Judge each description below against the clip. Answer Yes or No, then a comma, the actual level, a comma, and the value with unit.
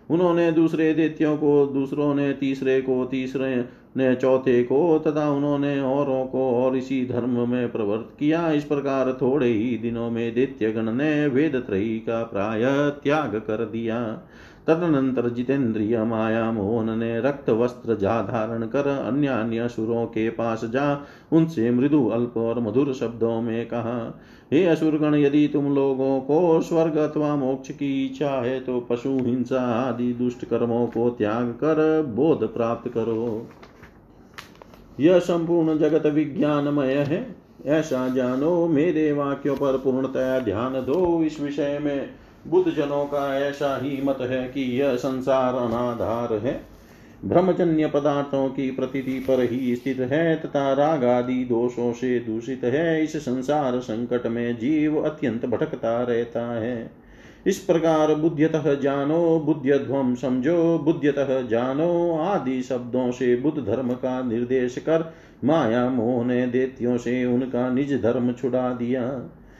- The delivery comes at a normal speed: Yes, average, 130 wpm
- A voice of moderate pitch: No, low, 130 Hz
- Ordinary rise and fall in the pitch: Yes, average, 3.3 semitones